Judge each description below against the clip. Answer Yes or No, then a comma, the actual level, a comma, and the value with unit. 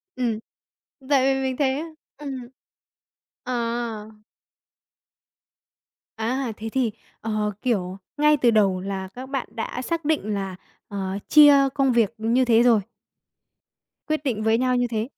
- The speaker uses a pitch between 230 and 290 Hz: Yes, high, 240 Hz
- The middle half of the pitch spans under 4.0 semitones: Yes, average, 3.6 semitones